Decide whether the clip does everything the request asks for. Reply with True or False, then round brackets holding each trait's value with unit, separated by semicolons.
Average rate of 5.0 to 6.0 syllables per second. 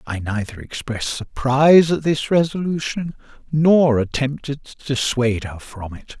False (4.6 syllables/s)